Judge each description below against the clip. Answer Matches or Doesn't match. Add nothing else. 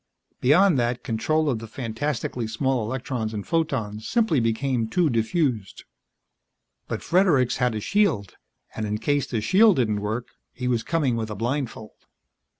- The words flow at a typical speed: Matches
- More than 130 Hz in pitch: Doesn't match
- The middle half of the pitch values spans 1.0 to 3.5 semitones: Doesn't match